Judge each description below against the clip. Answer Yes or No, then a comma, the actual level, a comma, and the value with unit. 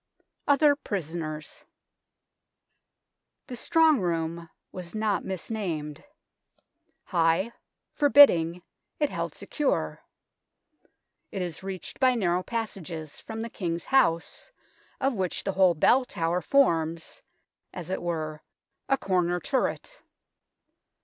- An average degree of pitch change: No, wide, 5.8 semitones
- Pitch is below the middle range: No, medium, 185 Hz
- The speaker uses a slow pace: Yes, slow, 110 wpm